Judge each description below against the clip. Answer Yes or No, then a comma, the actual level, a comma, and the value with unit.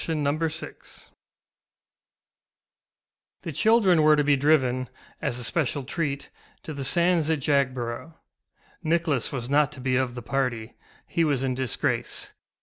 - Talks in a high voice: No, medium, 140 Hz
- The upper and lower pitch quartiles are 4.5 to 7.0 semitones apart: No, average, 3.6 semitones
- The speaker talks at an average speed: Yes, average, 145 wpm